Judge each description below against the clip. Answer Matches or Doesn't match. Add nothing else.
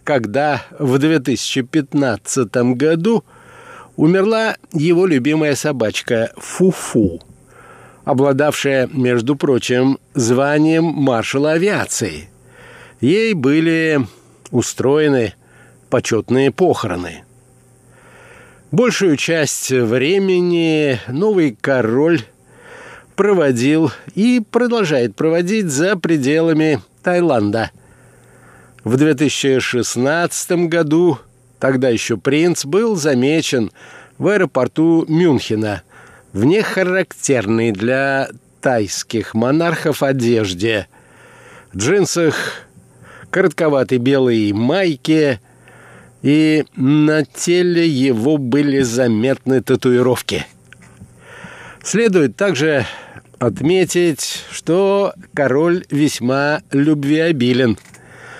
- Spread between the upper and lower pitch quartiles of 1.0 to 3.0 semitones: Doesn't match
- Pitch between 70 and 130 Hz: Doesn't match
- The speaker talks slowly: Matches